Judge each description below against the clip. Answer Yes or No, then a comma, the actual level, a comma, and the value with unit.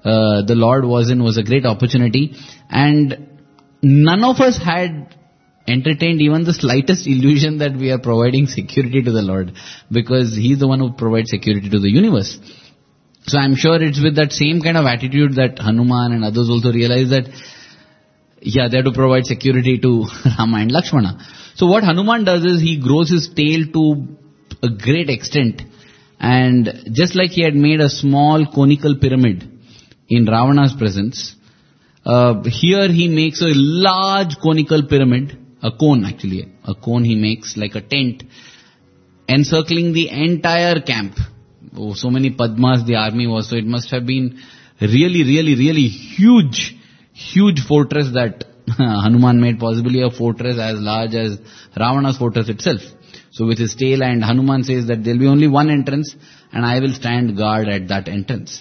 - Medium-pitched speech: No, low, 130 Hz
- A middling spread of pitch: Yes, average, 4.1 semitones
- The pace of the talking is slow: No, average, 170 wpm